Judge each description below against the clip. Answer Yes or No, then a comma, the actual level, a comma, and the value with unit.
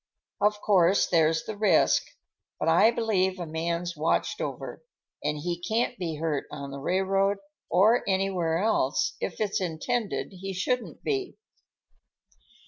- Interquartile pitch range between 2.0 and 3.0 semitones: No, average, 4.2 semitones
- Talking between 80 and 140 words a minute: Yes, slow, 135 wpm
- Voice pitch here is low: No, high, 190 Hz